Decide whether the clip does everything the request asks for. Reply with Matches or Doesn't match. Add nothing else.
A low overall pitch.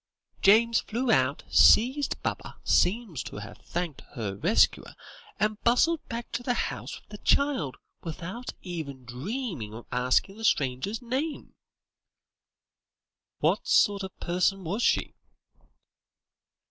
Doesn't match